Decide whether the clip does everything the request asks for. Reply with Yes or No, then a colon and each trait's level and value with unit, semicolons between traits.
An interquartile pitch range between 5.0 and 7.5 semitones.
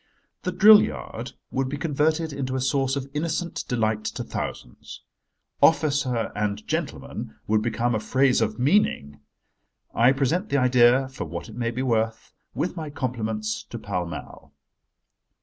No: average, 4.5 semitones